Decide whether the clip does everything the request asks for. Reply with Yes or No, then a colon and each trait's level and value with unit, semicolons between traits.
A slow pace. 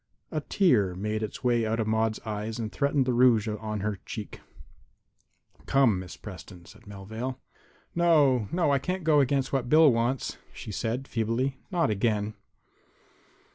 No: average, 155 wpm